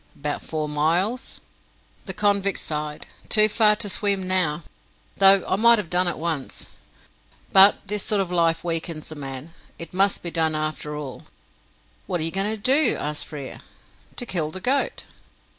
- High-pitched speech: No, medium, 180 Hz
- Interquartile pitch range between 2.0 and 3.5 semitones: No, average, 4.6 semitones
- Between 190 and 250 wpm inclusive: No, average, 170 wpm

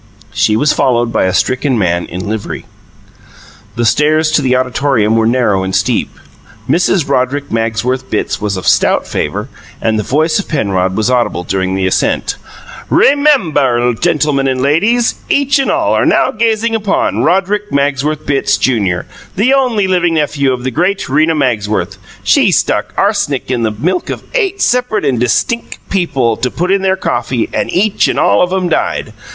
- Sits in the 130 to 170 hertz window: Yes, medium, 140 Hz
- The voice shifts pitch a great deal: Yes, wide, 8.2 semitones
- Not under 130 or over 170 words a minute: No, average, 180 wpm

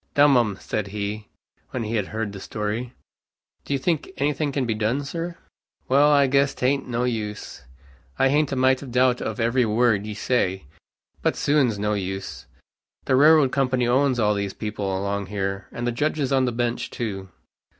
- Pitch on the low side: Yes, low, 120 Hz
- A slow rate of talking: No, average, 190 wpm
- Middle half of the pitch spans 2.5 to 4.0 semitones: No, average, 4.6 semitones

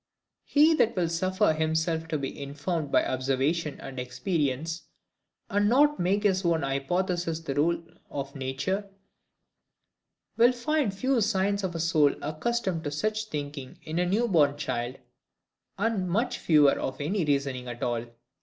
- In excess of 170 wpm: No, average, 150 wpm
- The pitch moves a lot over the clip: Yes, wide, 5.8 semitones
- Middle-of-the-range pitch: Yes, medium, 165 Hz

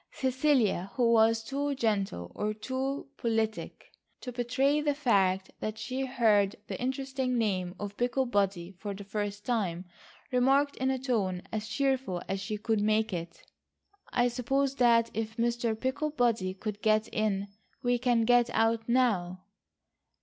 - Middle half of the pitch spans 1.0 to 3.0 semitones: No, average, 3.9 semitones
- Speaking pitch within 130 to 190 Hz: No, high, 225 Hz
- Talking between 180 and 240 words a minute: No, average, 145 wpm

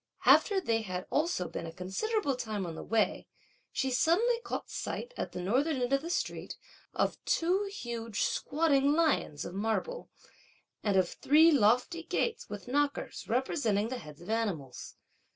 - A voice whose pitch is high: Yes, very high, 250 Hz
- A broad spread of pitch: Yes, wide, 8.1 semitones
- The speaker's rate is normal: Yes, average, 160 wpm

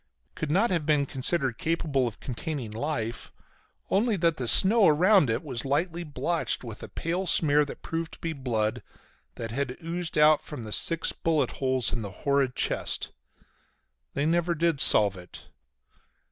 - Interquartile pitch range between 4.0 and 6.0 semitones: Yes, average, 4.8 semitones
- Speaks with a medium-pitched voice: Yes, medium, 150 Hz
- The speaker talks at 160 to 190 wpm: Yes, average, 165 wpm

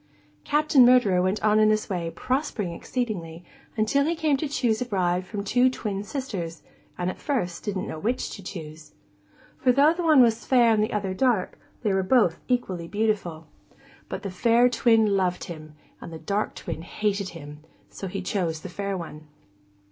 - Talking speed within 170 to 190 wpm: Yes, average, 180 wpm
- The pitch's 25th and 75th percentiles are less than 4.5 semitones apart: No, wide, 5.5 semitones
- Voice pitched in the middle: No, high, 205 Hz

